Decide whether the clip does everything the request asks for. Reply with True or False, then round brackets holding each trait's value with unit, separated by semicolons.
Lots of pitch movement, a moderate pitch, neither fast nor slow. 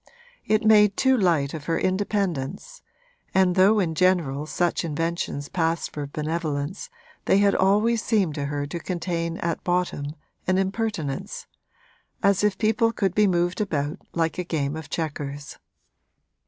False (4.6 semitones; 175 Hz; 145 wpm)